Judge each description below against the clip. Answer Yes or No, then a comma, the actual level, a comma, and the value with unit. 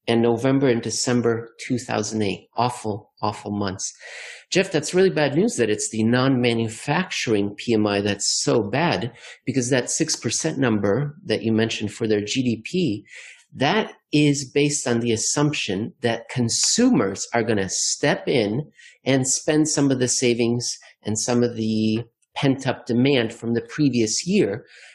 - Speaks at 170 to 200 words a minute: No, average, 145 wpm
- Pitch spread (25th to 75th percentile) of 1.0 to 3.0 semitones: No, average, 4.3 semitones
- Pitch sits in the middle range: No, low, 120 Hz